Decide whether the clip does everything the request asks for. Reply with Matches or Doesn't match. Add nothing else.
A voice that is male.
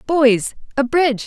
Doesn't match